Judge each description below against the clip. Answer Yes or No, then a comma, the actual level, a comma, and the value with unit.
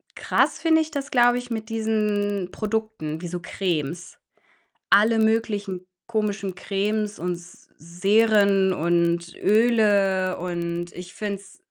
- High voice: Yes, high, 200 Hz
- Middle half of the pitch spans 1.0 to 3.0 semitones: No, average, 3.7 semitones